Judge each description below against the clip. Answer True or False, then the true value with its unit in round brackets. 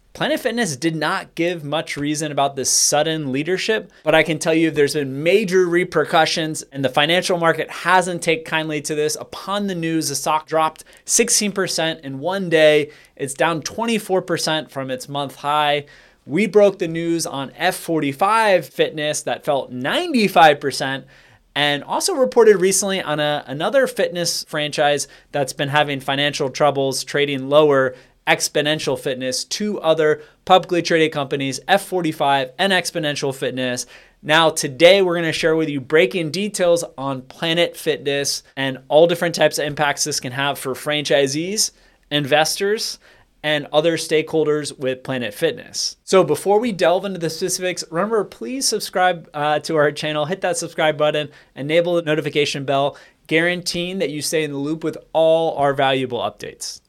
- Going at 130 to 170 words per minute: True (155 wpm)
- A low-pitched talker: False (155 Hz)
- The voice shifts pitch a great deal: False (3.7 semitones)